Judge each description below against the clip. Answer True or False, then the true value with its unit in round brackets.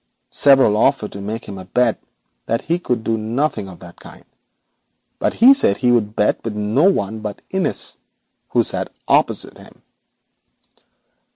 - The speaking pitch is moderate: False (110 Hz)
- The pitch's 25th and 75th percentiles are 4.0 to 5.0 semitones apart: True (4.4 semitones)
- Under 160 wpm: True (145 wpm)